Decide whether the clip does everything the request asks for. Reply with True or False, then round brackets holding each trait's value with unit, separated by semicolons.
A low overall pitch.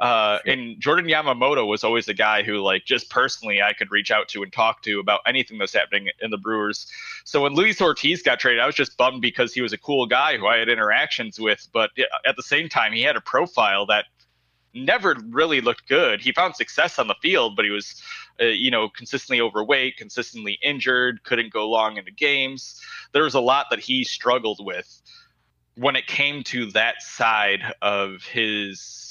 True (115 Hz)